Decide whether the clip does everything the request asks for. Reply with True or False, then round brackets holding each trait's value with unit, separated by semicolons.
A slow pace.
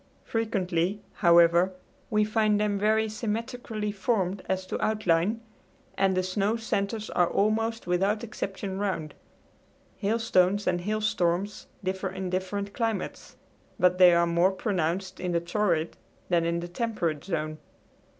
True (130 wpm)